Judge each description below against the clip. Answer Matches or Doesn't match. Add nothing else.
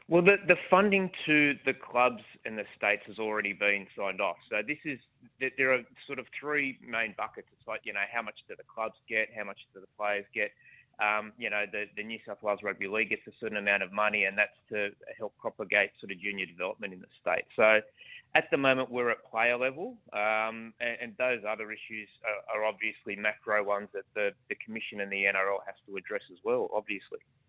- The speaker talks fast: Matches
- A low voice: Matches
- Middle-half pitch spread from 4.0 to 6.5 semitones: Matches